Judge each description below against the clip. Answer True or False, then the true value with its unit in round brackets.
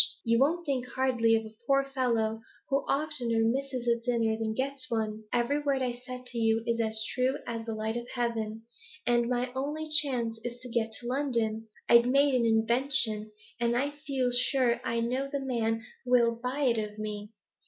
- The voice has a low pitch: False (240 Hz)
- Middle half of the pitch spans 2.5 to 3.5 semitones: True (2.8 semitones)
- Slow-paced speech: False (190 wpm)